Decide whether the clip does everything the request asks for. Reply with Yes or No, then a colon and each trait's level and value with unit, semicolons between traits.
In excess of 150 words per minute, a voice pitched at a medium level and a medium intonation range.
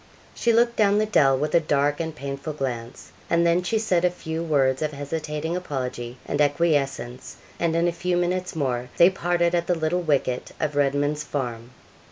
Yes: average, 190 wpm; medium, 155 Hz; average, 4.0 semitones